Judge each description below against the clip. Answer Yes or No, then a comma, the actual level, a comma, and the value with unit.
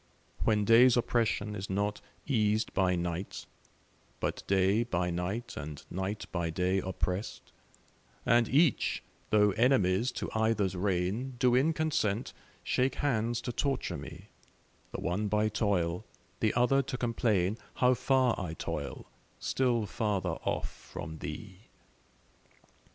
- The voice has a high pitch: No, low, 105 Hz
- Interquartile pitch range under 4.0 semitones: No, average, 4.6 semitones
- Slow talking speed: Yes, slow, 130 wpm